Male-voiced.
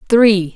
No: female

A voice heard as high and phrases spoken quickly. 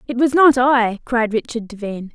No: high, 240 Hz; average, 195 wpm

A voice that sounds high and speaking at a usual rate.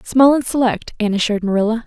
Yes: high, 225 Hz; average, 195 wpm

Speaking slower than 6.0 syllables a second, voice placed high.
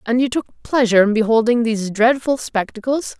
Yes: 5.5 syllables/s; high, 235 Hz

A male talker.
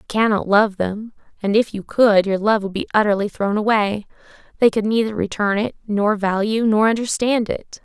No: female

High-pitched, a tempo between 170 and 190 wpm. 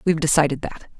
No: medium, 155 Hz; average, 180 wpm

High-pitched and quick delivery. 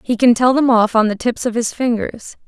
Yes: high, 235 Hz; fast, 265 wpm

